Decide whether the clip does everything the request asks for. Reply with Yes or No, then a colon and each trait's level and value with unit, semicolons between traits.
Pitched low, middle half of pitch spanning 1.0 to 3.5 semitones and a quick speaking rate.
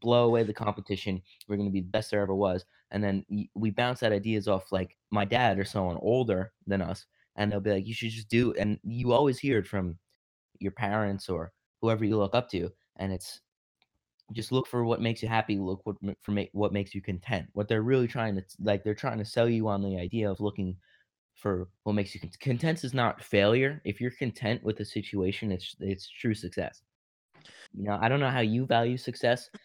Yes: low, 105 Hz; average, 2.8 semitones; fast, 225 wpm